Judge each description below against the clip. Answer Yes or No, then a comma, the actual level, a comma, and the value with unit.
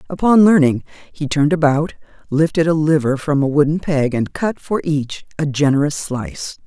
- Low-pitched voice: No, medium, 150 Hz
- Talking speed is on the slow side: No, average, 170 wpm